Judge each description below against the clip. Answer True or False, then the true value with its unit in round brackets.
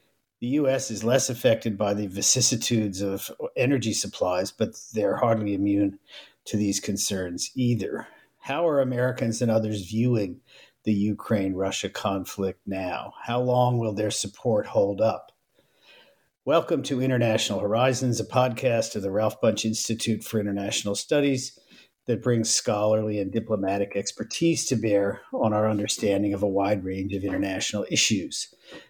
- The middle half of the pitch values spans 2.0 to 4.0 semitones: True (3.3 semitones)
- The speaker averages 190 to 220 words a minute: False (145 wpm)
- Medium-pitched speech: False (110 Hz)